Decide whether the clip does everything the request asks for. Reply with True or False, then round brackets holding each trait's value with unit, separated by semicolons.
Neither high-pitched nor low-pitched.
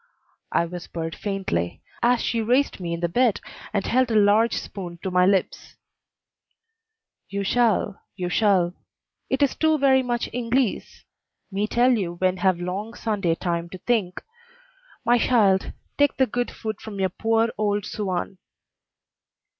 False (205 Hz)